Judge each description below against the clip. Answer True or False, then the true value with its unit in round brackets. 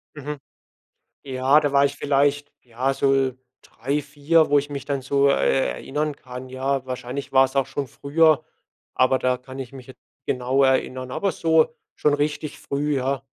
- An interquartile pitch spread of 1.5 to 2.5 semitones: True (1.9 semitones)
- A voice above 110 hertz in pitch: True (140 Hz)